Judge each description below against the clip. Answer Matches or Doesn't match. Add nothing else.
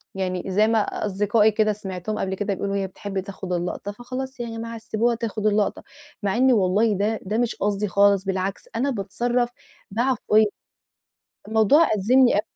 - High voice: Matches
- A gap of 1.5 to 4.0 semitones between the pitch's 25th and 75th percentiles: Matches